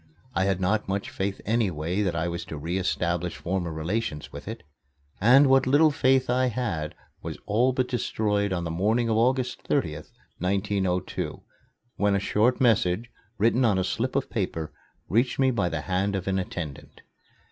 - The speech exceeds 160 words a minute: Yes, average, 175 wpm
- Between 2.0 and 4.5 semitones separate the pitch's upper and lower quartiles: No, average, 5.1 semitones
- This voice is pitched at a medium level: No, low, 100 Hz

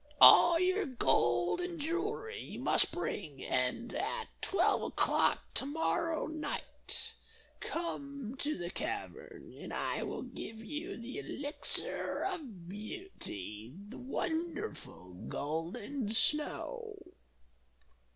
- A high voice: Yes, very high, 285 Hz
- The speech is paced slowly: Yes, slow, 105 wpm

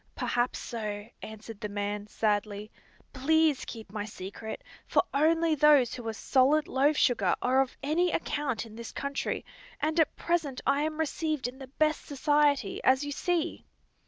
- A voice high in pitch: Yes, very high, 265 Hz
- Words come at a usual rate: Yes, average, 160 wpm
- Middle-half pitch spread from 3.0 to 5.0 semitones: No, wide, 5.6 semitones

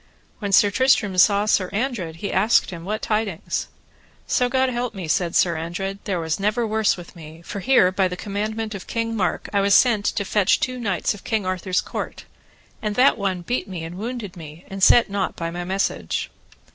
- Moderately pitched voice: No, high, 200 Hz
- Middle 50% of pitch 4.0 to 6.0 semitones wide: No, average, 3.3 semitones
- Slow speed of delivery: No, fast, 205 wpm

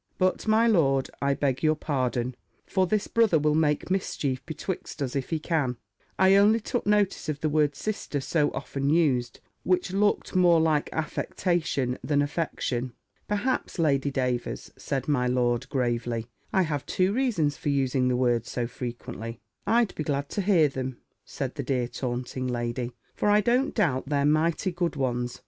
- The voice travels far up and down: Yes, wide, 5.9 semitones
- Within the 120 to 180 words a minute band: Yes, average, 170 wpm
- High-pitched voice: No, medium, 145 Hz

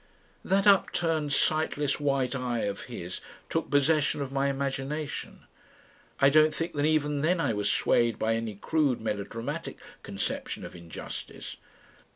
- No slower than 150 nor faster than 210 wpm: No, average, 140 wpm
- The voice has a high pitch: No, medium, 140 Hz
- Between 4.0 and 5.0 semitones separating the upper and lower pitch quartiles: Yes, average, 4.6 semitones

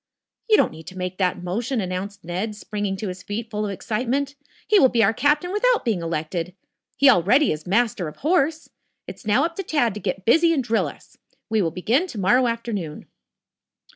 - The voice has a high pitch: Yes, high, 215 Hz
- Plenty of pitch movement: Yes, wide, 6.4 semitones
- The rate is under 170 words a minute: No, average, 200 wpm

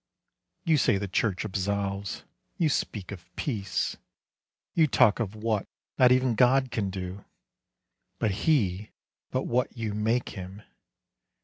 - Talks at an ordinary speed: No, slow, 130 wpm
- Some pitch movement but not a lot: Yes, average, 4.1 semitones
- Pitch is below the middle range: Yes, low, 105 Hz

